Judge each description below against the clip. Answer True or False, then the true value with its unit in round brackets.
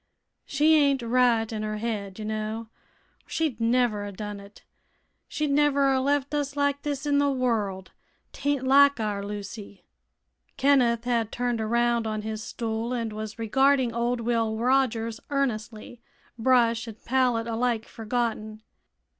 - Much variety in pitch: False (3.5 semitones)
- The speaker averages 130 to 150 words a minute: True (145 wpm)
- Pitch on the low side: False (235 Hz)